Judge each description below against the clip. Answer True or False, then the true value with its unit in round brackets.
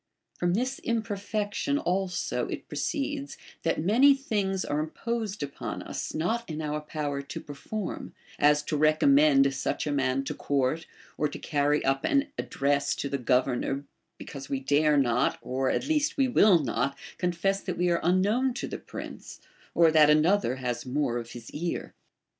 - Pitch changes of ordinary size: False (6.5 semitones)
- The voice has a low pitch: False (155 Hz)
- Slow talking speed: False (165 wpm)